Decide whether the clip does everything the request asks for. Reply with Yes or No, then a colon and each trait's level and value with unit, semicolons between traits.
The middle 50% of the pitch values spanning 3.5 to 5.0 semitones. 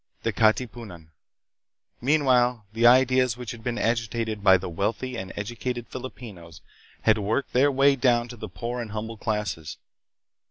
No: average, 2.9 semitones